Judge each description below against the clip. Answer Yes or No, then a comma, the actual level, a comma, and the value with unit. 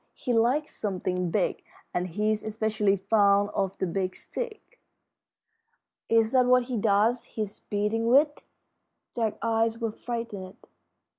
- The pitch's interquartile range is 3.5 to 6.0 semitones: No, average, 2.8 semitones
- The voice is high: Yes, high, 220 Hz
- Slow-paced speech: Yes, slow, 130 wpm